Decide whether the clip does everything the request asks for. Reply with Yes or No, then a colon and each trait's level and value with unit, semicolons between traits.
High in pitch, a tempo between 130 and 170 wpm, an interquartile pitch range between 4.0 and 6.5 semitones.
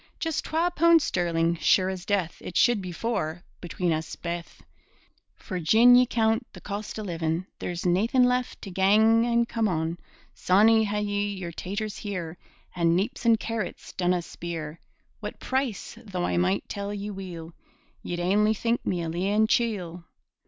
Yes: high, 195 Hz; average, 165 wpm; average, 4.3 semitones